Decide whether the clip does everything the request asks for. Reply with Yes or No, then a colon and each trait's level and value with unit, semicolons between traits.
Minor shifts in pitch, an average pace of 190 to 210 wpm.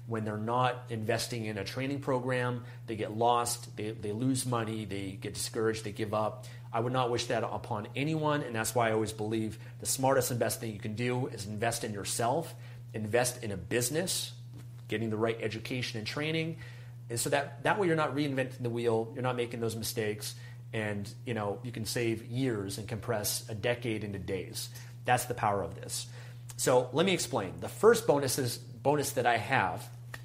Yes: narrow, 2.0 semitones; average, 200 wpm